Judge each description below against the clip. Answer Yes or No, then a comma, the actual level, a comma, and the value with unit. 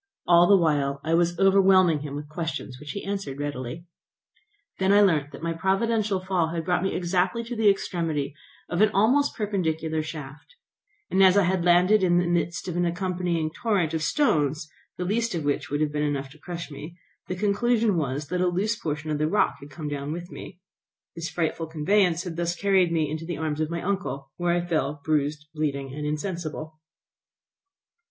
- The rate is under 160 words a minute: No, average, 195 wpm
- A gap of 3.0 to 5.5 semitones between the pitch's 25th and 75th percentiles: Yes, average, 3.8 semitones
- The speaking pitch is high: No, medium, 170 Hz